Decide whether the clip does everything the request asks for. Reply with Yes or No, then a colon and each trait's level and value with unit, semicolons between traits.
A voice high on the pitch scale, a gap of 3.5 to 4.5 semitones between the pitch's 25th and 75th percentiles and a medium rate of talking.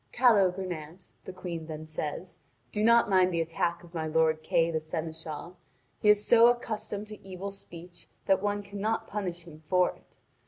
No: medium, 180 Hz; average, 4.0 semitones; average, 170 wpm